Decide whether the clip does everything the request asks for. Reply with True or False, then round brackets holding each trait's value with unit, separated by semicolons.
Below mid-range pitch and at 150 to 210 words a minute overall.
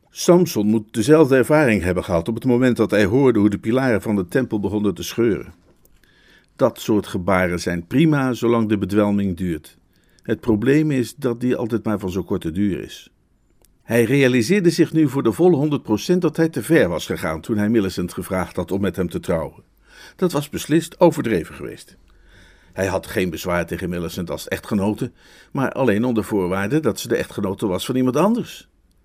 True (110 Hz; 190 wpm)